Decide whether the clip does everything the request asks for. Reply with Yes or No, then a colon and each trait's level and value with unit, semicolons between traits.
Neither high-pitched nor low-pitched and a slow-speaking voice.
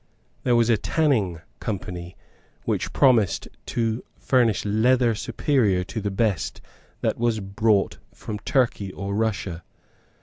No: low, 110 Hz; slow, 125 wpm